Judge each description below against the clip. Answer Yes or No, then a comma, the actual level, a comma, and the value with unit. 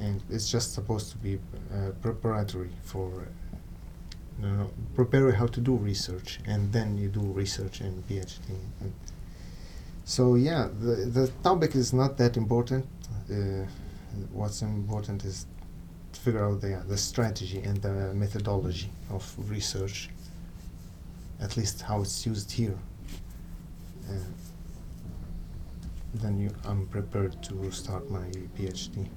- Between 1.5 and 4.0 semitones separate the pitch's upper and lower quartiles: Yes, average, 2.9 semitones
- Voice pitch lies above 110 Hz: No, low, 100 Hz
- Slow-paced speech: Yes, slow, 130 wpm